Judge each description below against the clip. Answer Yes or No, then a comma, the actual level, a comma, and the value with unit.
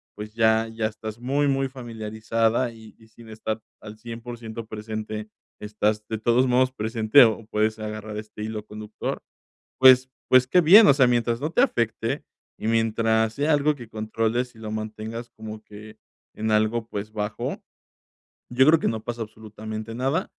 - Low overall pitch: Yes, low, 110 Hz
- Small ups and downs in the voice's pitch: Yes, narrow, 2.1 semitones